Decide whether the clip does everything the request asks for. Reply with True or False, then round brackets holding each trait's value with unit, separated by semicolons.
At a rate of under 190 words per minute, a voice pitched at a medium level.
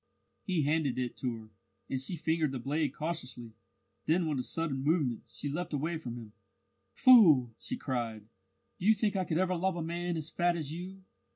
False (195 wpm; 155 Hz)